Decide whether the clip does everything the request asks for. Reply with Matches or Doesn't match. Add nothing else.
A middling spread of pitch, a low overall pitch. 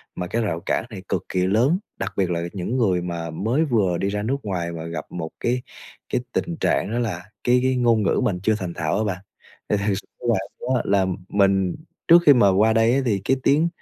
Matches